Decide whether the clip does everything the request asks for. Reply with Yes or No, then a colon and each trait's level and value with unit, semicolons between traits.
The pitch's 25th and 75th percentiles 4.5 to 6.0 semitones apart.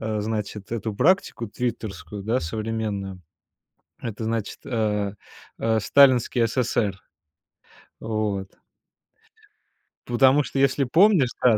No: average, 3.0 semitones